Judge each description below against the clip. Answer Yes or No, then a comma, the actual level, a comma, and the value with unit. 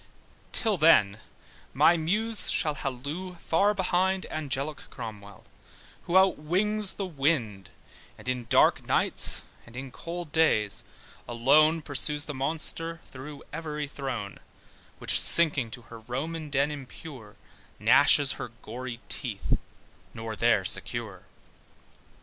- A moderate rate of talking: No, slow, 115 wpm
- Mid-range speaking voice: Yes, medium, 145 Hz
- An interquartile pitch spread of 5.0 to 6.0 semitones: Yes, average, 5.3 semitones